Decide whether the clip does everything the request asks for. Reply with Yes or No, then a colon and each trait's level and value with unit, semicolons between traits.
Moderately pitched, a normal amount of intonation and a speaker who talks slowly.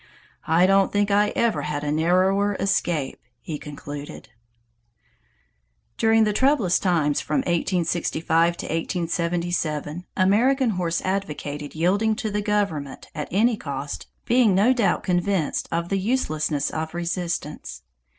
Yes: medium, 175 Hz; average, 4.4 semitones; slow, 125 wpm